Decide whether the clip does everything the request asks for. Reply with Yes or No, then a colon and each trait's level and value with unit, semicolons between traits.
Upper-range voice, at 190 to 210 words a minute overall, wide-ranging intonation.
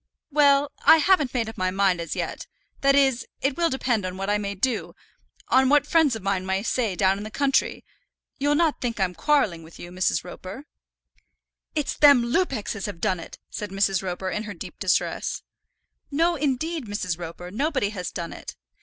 Yes: high, 220 Hz; average, 200 wpm; wide, 6.8 semitones